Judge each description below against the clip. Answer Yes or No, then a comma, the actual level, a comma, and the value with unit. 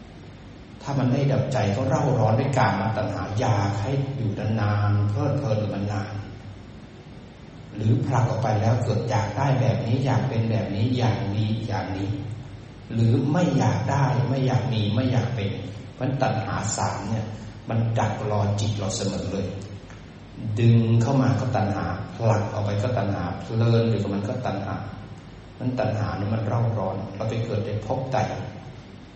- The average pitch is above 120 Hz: No, low, 110 Hz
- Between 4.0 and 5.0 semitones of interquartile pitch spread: No, average, 3.6 semitones